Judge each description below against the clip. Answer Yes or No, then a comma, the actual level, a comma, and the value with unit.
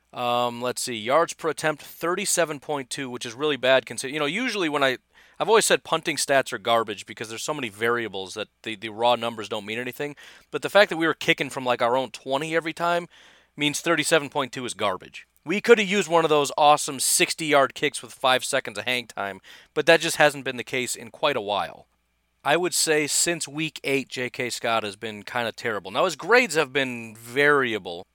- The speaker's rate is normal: No, fast, 215 wpm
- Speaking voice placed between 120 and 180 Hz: Yes, low, 135 Hz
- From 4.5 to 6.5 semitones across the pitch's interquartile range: Yes, average, 4.8 semitones